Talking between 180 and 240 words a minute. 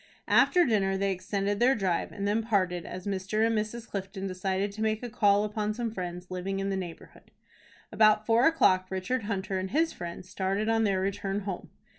Yes: average, 195 wpm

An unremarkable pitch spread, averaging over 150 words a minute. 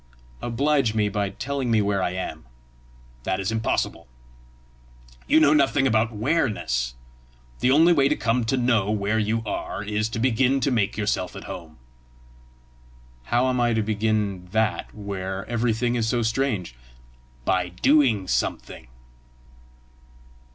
No: average, 3.8 semitones; average, 140 wpm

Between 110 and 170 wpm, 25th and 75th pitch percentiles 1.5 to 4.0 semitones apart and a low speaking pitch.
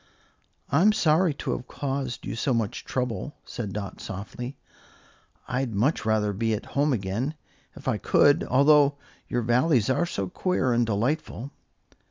No: average, 150 wpm; average, 4.7 semitones; low, 125 Hz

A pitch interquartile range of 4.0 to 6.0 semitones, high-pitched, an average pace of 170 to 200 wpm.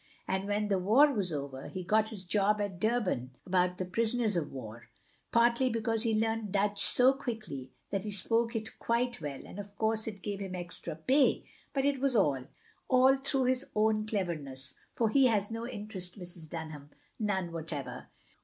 Yes: average, 4.4 semitones; high, 205 Hz; average, 185 wpm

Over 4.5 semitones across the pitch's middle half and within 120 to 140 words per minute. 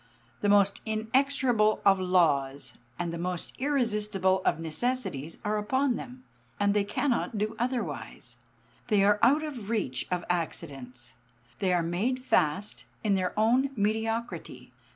Yes: average, 5.2 semitones; slow, 135 wpm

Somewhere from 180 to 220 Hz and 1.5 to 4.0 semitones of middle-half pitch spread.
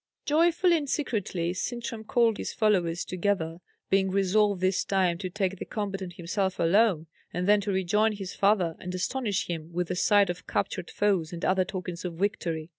Yes: high, 190 Hz; average, 2.8 semitones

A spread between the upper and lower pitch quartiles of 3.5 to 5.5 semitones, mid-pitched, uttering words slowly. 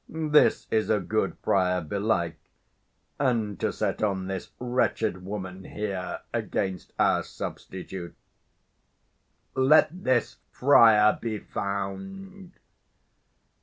No: average, 5.1 semitones; low, 105 Hz; slow, 90 wpm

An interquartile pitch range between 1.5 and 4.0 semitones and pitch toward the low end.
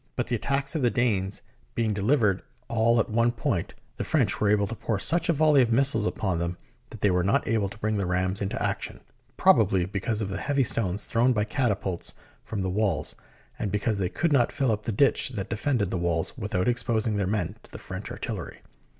Yes: average, 3.6 semitones; low, 105 Hz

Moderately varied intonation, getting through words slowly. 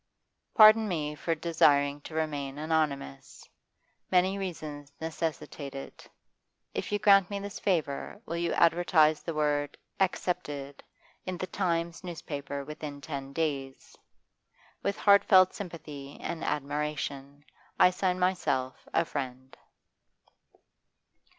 Yes: average, 4.0 semitones; slow, 110 wpm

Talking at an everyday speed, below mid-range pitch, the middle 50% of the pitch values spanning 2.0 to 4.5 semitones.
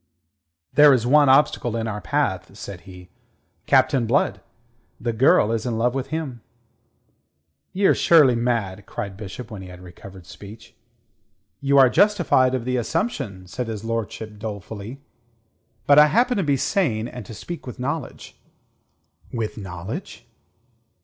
No: average, 145 wpm; low, 120 Hz; average, 4.9 semitones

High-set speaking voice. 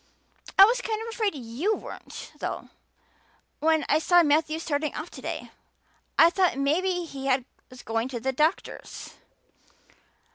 Yes: very high, 315 Hz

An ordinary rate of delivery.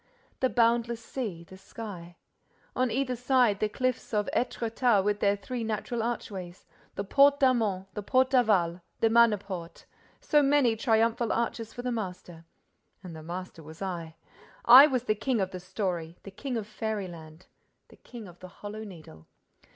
Yes: average, 155 wpm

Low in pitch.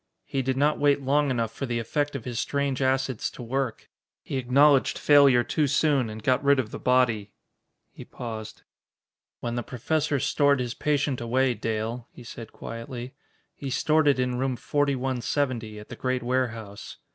Yes: low, 130 Hz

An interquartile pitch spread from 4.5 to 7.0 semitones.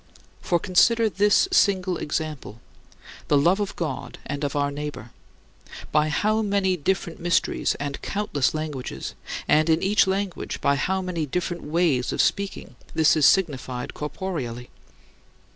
Yes: average, 4.9 semitones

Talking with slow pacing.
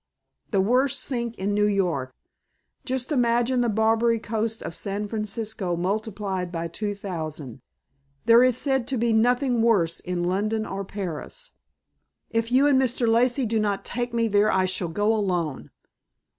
No: average, 155 wpm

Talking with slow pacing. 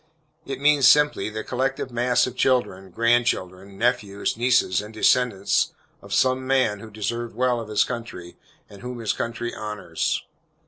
No: average, 155 wpm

